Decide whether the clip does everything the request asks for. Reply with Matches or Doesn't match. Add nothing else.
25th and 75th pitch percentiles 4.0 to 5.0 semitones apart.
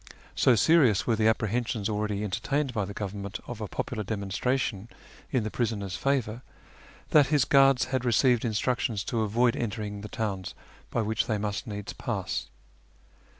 Doesn't match